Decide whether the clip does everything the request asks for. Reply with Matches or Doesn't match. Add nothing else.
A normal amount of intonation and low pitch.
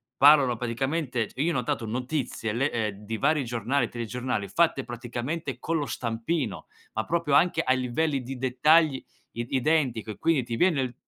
Matches